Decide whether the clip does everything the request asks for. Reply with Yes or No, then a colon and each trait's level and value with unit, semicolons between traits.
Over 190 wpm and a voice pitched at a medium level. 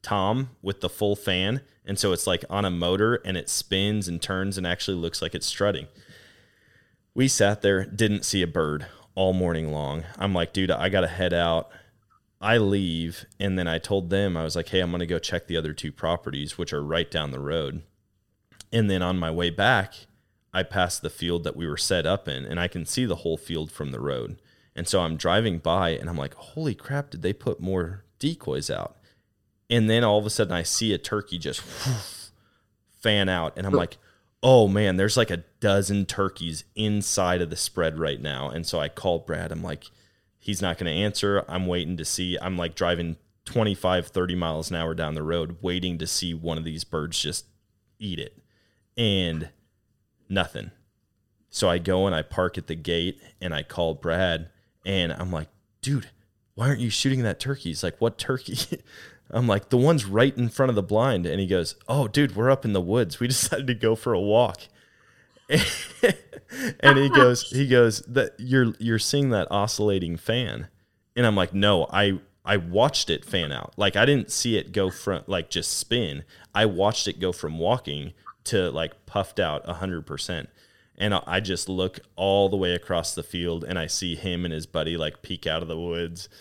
No: fast, 205 wpm; very low, 95 Hz